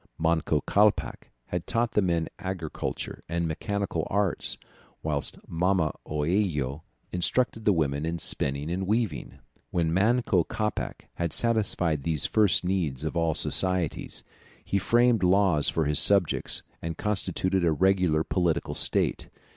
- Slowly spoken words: Yes, slow, 130 wpm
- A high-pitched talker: No, very low, 90 Hz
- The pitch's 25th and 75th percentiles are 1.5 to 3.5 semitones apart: No, average, 3.9 semitones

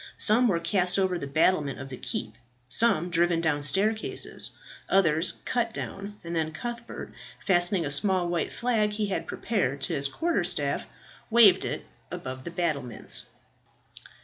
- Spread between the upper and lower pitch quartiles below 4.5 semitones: No, average, 5.3 semitones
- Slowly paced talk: No, average, 150 wpm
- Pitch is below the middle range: No, medium, 175 Hz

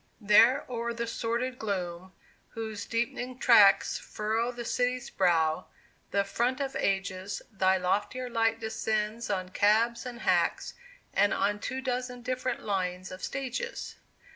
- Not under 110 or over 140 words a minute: Yes, slow, 135 wpm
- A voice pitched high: Yes, high, 225 Hz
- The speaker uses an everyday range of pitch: Yes, average, 3.9 semitones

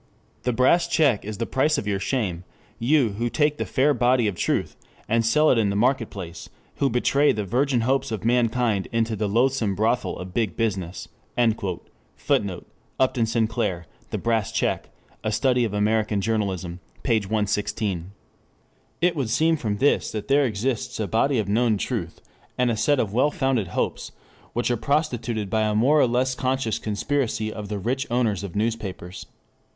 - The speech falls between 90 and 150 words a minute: No, average, 175 wpm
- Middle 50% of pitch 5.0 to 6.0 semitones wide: No, average, 3.9 semitones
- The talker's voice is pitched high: No, low, 115 Hz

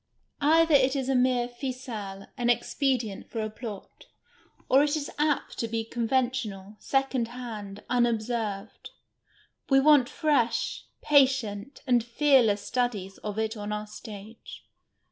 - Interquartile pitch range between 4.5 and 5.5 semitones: No, average, 3.8 semitones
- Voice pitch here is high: Yes, high, 240 Hz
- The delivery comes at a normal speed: No, slow, 130 wpm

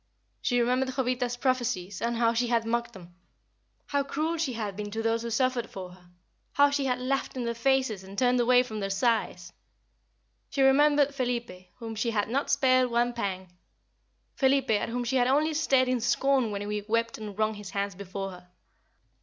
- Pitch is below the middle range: No, high, 235 Hz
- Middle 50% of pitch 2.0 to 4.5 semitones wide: Yes, average, 3.7 semitones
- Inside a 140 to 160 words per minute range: No, average, 195 wpm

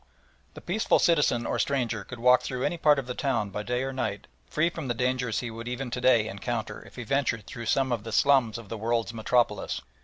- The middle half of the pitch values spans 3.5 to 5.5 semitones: No, average, 2.8 semitones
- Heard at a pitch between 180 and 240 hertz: No, low, 120 Hz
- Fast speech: Yes, fast, 235 wpm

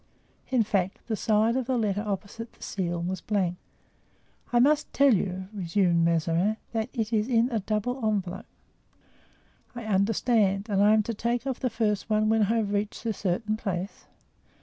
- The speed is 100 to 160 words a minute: No, average, 175 wpm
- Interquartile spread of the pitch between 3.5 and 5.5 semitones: No, average, 2.9 semitones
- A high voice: Yes, high, 215 Hz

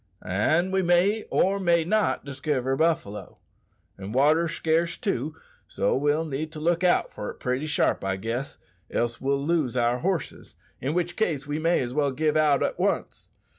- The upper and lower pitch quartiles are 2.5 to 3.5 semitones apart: No, average, 4.5 semitones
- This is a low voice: No, medium, 155 Hz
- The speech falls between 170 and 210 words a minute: Yes, average, 175 wpm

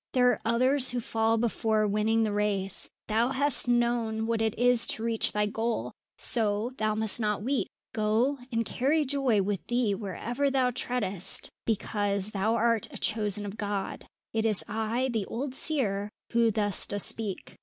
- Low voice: No, high, 225 Hz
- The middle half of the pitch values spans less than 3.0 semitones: Yes, narrow, 2.5 semitones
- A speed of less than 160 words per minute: No, average, 170 wpm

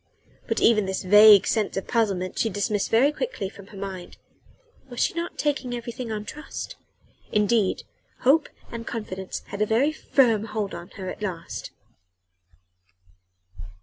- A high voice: Yes, high, 215 Hz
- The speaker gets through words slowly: No, average, 150 wpm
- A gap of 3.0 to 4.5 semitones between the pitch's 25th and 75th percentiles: Yes, average, 3.3 semitones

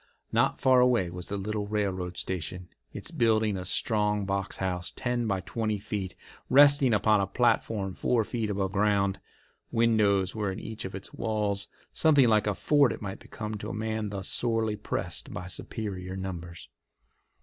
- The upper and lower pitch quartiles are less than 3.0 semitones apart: Yes, narrow, 2.6 semitones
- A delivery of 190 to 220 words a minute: No, average, 170 wpm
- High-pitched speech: No, low, 105 Hz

